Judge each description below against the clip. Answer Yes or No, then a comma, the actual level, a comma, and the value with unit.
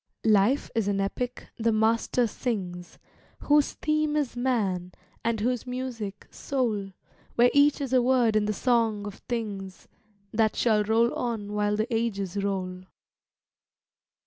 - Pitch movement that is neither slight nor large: Yes, average, 3.5 semitones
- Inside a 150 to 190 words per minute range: No, average, 140 wpm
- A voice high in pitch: Yes, high, 225 Hz